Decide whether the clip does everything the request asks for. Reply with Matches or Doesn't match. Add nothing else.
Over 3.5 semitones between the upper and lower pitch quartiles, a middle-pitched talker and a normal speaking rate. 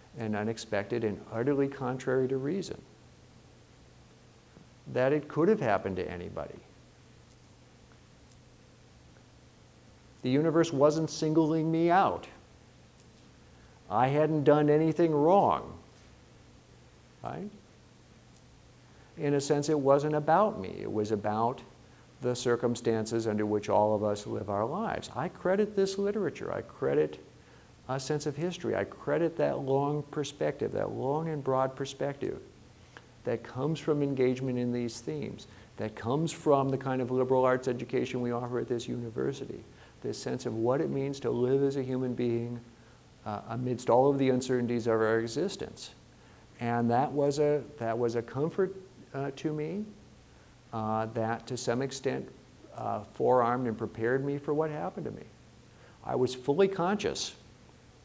Doesn't match